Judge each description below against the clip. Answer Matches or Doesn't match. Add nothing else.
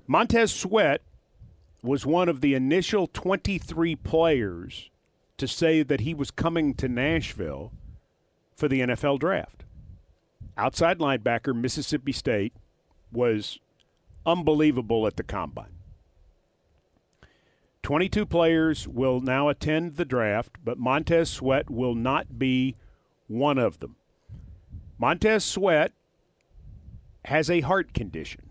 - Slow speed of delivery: Matches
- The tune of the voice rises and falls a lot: Matches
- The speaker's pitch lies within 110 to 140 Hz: Matches